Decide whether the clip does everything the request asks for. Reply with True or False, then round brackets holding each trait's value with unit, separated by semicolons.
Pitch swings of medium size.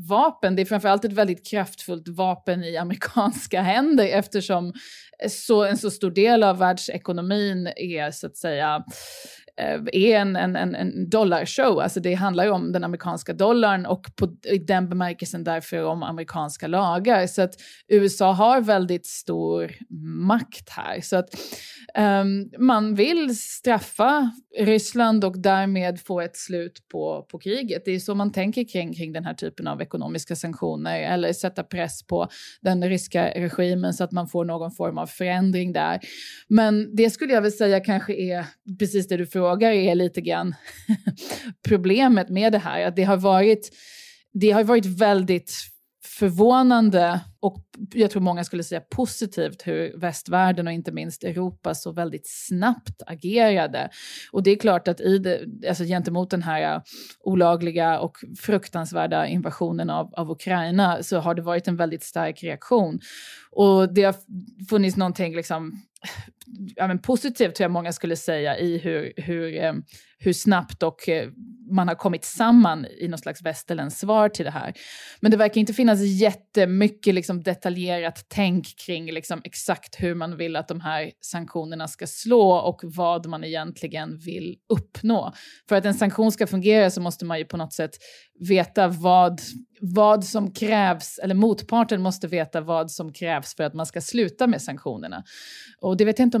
True (3.4 semitones)